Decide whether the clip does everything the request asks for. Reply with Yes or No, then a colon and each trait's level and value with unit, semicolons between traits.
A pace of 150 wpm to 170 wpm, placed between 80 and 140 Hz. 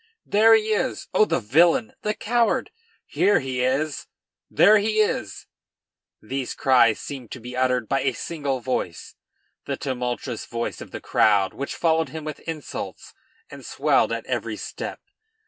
Yes: average, 155 wpm; low, 135 Hz